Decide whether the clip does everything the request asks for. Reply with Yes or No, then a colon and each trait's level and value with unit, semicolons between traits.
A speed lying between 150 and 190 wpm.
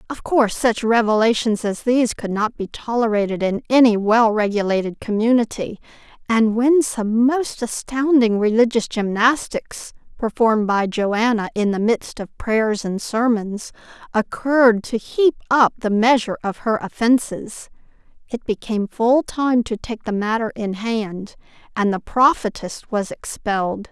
No: average, 140 wpm